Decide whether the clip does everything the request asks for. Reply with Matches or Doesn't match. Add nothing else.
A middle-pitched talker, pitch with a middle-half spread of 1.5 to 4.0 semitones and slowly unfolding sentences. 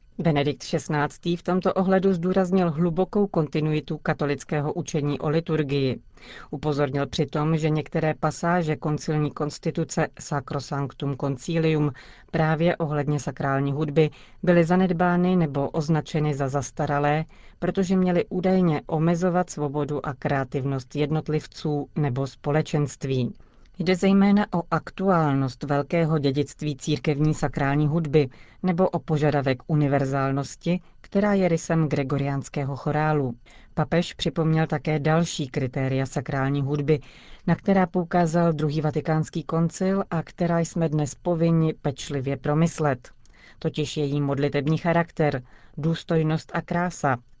Matches